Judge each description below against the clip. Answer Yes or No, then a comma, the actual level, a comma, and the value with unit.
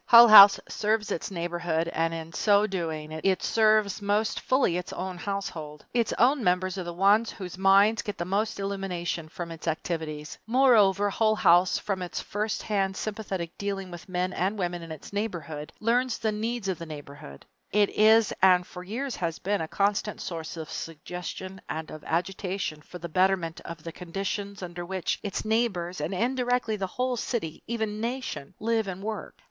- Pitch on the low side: No, high, 190 Hz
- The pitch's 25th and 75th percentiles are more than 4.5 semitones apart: No, average, 3.8 semitones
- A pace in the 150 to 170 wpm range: No, average, 180 wpm